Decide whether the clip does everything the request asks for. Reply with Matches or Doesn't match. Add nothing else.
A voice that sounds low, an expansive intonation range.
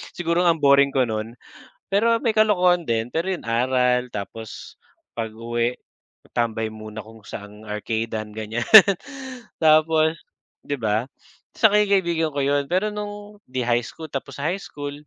Matches